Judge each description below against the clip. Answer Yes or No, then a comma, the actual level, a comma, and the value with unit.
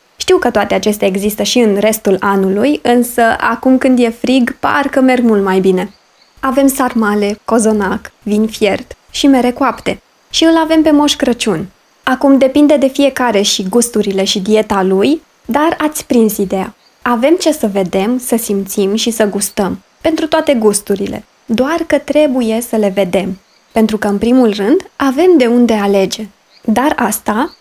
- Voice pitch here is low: No, high, 230 Hz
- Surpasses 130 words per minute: Yes, average, 165 wpm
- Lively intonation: No, average, 4.9 semitones